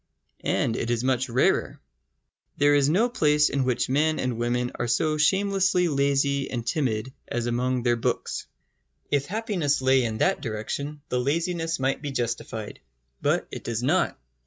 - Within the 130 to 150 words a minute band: No, average, 160 wpm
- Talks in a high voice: No, low, 135 Hz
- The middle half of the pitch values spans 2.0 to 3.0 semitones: No, average, 4.1 semitones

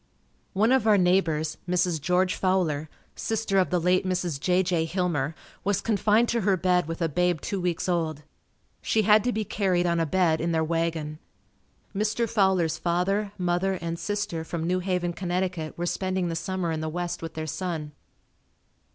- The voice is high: No, medium, 180 Hz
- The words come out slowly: No, average, 180 wpm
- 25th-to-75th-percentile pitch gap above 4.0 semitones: No, narrow, 2.5 semitones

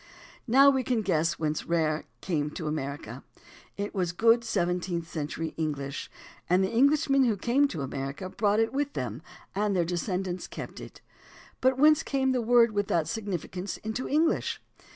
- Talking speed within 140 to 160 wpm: No, average, 170 wpm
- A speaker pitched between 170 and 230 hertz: Yes, high, 190 Hz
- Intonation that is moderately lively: No, wide, 7.0 semitones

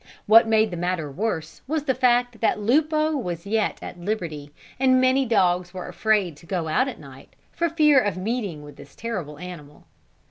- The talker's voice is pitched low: No, high, 210 Hz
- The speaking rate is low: No, average, 185 wpm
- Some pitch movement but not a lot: No, wide, 6.7 semitones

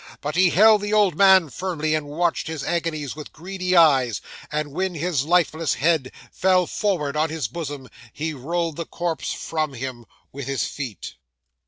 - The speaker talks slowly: No, average, 170 wpm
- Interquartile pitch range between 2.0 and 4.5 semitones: Yes, average, 3.6 semitones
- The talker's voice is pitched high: No, medium, 160 Hz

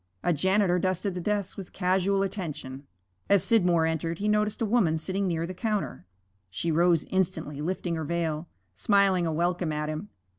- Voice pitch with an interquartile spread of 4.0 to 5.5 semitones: No, average, 3.4 semitones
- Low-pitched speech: No, medium, 180 Hz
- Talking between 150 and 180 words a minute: Yes, average, 175 wpm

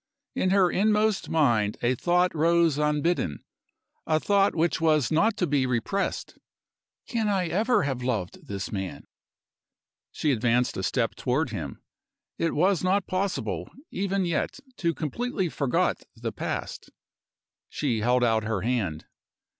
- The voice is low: No, medium, 155 Hz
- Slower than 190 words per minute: Yes, average, 140 wpm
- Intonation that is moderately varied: No, wide, 7.4 semitones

